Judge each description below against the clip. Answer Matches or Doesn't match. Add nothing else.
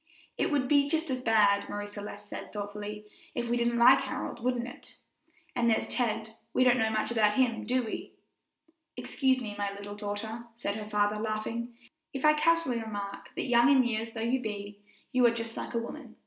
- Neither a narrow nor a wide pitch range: Matches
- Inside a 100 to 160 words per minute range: Doesn't match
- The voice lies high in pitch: Matches